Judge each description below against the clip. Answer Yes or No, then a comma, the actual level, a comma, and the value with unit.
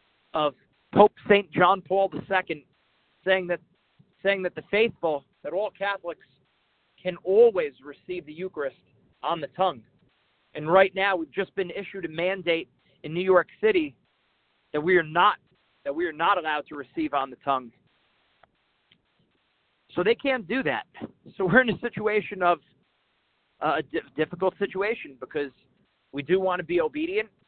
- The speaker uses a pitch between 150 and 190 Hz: Yes, medium, 185 Hz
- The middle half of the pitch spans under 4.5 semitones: Yes, average, 3.9 semitones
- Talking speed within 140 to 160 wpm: Yes, average, 155 wpm